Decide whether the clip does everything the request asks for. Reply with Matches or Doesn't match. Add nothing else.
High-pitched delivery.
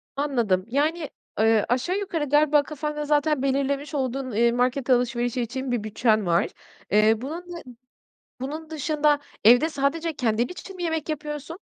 Matches